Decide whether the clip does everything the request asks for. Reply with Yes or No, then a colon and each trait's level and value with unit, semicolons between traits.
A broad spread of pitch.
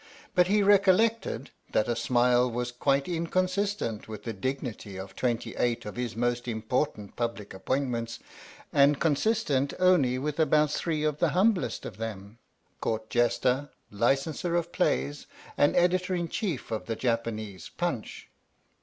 Yes: wide, 6.6 semitones